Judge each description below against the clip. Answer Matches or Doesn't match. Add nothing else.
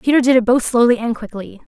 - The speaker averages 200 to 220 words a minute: Doesn't match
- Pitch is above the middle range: Matches